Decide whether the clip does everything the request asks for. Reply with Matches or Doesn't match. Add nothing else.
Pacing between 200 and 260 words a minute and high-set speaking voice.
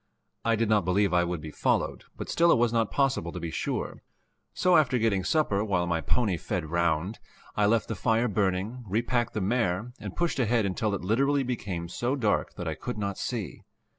Doesn't match